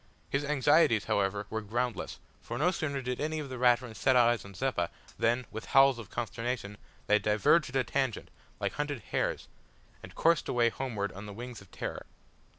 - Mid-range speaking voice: No, low, 120 Hz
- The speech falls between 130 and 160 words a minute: No, average, 185 wpm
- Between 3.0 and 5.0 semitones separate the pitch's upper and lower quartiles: Yes, average, 4.3 semitones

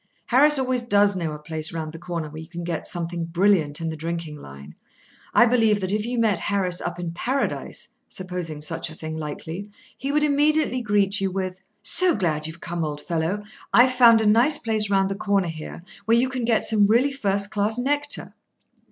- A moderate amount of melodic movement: No, wide, 6.0 semitones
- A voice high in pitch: Yes, high, 195 Hz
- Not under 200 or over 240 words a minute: Yes, fast, 205 wpm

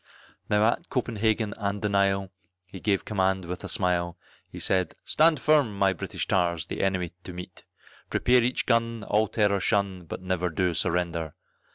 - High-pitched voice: No, very low, 95 Hz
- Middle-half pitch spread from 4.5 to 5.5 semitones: No, average, 3.1 semitones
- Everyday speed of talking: Yes, average, 170 wpm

